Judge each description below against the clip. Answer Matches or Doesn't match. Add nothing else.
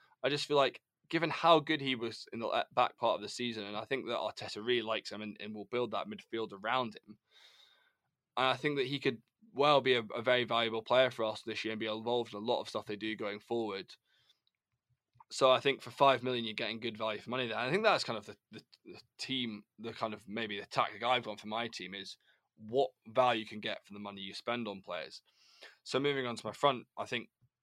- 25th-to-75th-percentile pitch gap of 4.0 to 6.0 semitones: Doesn't match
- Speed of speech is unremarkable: Doesn't match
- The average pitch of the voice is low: Matches